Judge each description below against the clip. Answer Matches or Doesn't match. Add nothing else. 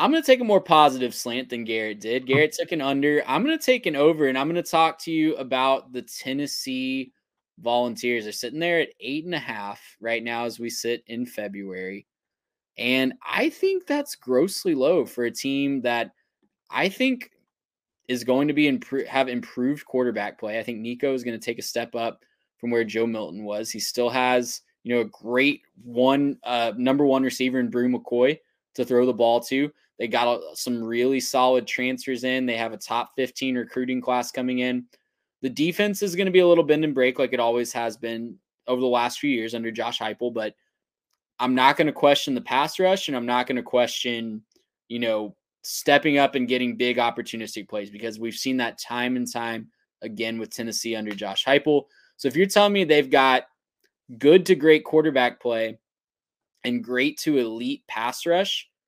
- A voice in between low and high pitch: Doesn't match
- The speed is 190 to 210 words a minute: Matches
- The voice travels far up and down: Doesn't match